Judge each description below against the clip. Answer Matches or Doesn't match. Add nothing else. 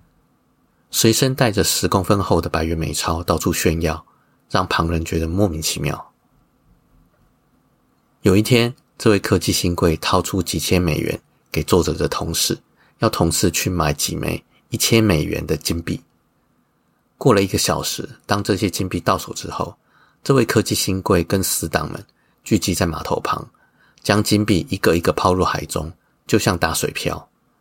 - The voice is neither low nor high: Doesn't match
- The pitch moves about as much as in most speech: Matches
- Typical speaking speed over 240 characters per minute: Doesn't match